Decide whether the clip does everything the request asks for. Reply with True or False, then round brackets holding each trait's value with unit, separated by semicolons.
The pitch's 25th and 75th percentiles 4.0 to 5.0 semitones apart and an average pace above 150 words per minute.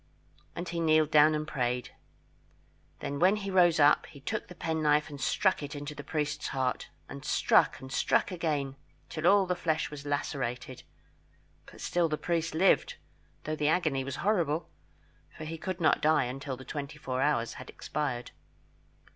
False (3.3 semitones; 170 wpm)